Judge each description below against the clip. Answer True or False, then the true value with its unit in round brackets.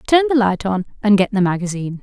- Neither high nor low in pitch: False (210 Hz)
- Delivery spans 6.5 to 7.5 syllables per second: True (6.7 syllables/s)